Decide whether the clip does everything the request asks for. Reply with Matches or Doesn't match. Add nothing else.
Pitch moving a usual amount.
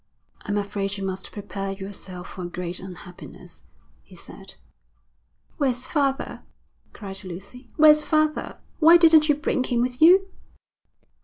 Doesn't match